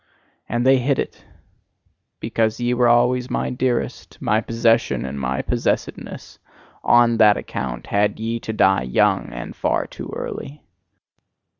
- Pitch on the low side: Yes, low, 115 Hz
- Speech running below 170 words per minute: Yes, average, 140 wpm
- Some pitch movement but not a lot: Yes, average, 3.3 semitones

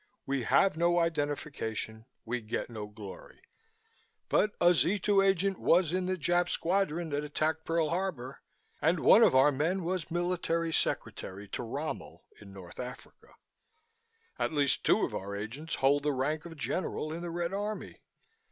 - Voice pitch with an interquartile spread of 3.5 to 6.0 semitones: Yes, average, 5.0 semitones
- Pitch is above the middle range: No, medium, 160 Hz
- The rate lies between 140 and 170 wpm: Yes, average, 160 wpm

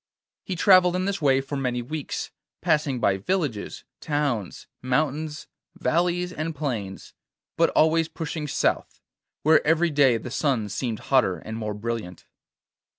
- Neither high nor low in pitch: Yes, medium, 145 Hz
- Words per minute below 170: Yes, average, 140 wpm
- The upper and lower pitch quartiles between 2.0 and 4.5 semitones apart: No, wide, 5.5 semitones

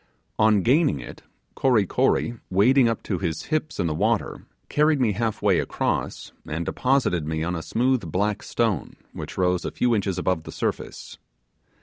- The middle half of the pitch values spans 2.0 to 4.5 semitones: No, wide, 5.6 semitones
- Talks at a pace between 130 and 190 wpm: Yes, average, 170 wpm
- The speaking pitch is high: No, low, 105 Hz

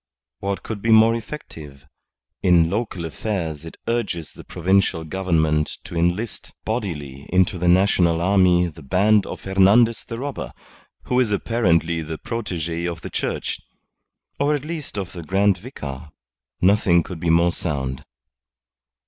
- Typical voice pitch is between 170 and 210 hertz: No, very low, 90 Hz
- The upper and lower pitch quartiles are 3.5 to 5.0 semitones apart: Yes, average, 4.5 semitones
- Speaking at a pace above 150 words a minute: No, average, 145 wpm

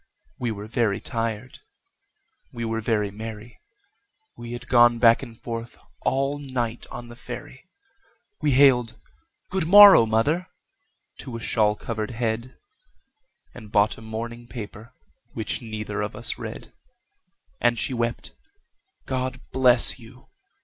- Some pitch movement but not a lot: No, narrow, 2.1 semitones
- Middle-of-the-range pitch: No, low, 115 Hz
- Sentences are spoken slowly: Yes, slow, 130 wpm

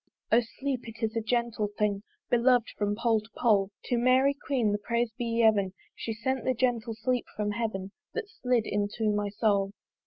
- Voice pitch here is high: Yes, high, 225 Hz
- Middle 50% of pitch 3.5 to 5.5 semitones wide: No, average, 2.8 semitones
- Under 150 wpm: No, average, 185 wpm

